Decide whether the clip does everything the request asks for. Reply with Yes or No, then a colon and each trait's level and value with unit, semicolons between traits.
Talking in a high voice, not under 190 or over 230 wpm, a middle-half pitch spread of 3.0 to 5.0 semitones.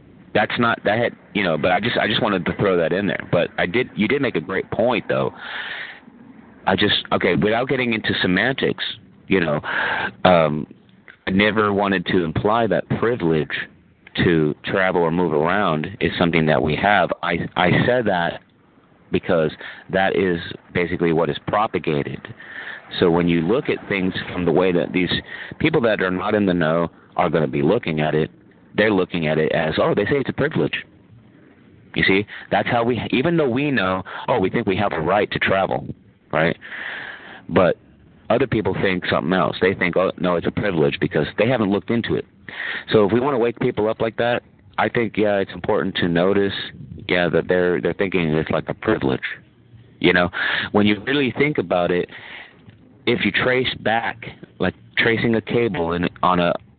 No: very low, 95 Hz; average, 195 wpm; average, 4.6 semitones